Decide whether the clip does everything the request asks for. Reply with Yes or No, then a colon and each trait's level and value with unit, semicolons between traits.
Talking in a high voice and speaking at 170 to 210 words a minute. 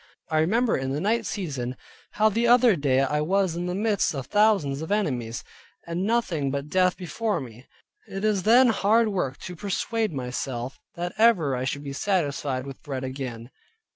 No: medium, 170 Hz; average, 180 wpm